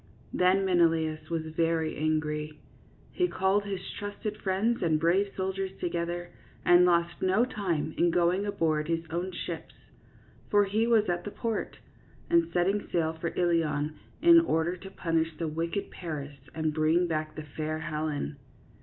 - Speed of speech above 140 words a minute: Yes, average, 160 wpm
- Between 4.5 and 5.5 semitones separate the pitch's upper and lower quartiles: No, average, 3.4 semitones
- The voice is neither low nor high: Yes, medium, 170 Hz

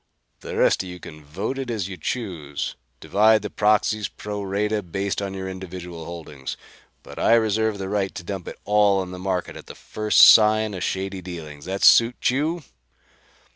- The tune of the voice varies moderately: Yes, average, 3.0 semitones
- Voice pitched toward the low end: Yes, very low, 95 Hz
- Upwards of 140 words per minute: Yes, average, 185 wpm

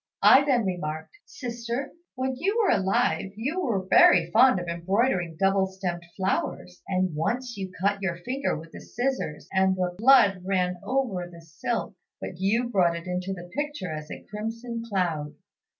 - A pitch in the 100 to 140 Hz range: No, high, 195 Hz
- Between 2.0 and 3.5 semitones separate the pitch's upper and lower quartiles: No, average, 5.3 semitones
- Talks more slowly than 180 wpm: Yes, average, 165 wpm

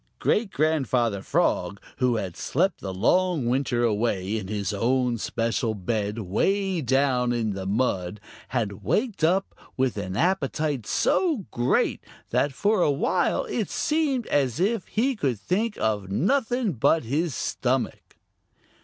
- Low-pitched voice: Yes, low, 130 Hz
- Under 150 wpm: Yes, average, 140 wpm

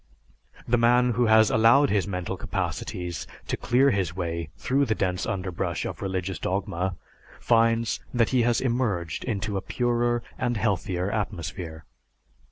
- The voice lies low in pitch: Yes, low, 105 Hz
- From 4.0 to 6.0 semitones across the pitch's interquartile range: Yes, average, 4.7 semitones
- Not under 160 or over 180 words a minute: No, average, 145 wpm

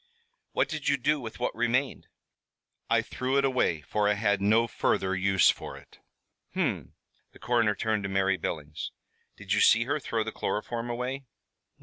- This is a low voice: Yes, low, 115 Hz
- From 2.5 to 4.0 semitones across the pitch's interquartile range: No, average, 4.5 semitones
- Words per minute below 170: No, average, 175 wpm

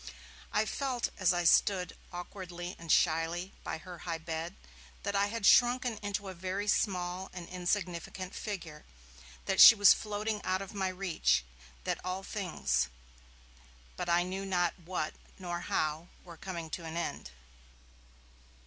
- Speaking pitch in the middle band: Yes, medium, 180 Hz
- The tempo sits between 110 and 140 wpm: No, average, 150 wpm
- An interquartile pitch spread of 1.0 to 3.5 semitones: Yes, narrow, 2.5 semitones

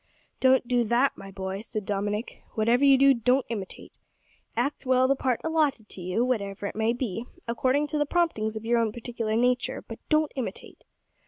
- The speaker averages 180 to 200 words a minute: Yes, average, 185 wpm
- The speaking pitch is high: Yes, high, 240 Hz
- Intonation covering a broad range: No, average, 3.6 semitones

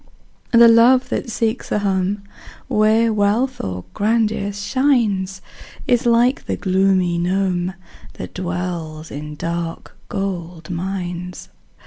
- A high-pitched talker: Yes, high, 195 Hz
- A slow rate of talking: Yes, slow, 110 wpm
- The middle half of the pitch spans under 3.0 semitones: No, average, 4.2 semitones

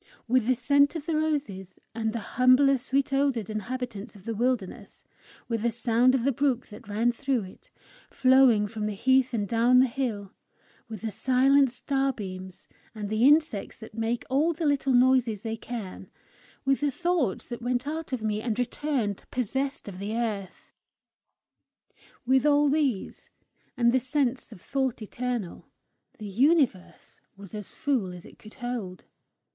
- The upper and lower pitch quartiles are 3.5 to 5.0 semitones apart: Yes, average, 3.9 semitones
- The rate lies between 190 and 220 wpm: No, average, 160 wpm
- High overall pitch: Yes, high, 245 Hz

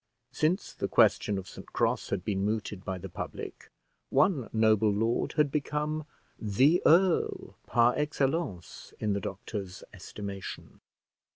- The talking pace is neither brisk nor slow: No, slow, 130 wpm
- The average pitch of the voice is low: Yes, low, 110 Hz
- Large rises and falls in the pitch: Yes, wide, 7.0 semitones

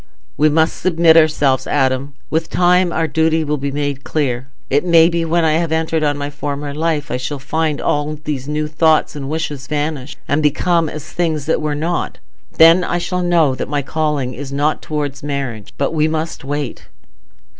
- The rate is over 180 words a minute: Yes, average, 190 wpm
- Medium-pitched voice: Yes, medium, 150 Hz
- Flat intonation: Yes, narrow, 2.1 semitones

